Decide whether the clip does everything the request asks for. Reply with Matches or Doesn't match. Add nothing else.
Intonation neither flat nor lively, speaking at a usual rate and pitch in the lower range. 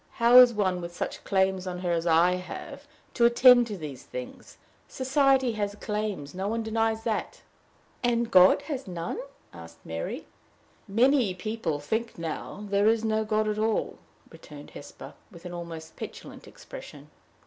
Doesn't match